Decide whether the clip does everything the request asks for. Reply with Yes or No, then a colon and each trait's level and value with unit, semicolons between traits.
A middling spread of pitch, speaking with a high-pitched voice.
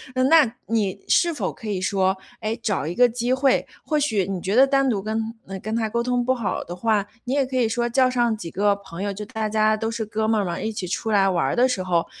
Yes: average, 3.7 semitones; high, 220 Hz